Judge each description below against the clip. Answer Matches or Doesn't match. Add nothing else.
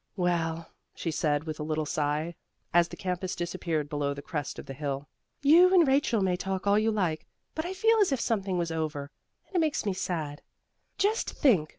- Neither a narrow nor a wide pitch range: Doesn't match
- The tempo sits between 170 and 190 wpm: Doesn't match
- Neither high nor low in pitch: Matches